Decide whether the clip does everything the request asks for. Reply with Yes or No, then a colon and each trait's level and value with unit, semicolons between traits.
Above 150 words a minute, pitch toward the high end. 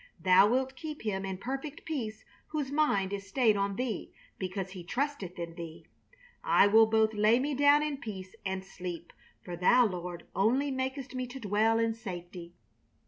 Yes: average, 175 wpm; high, 215 Hz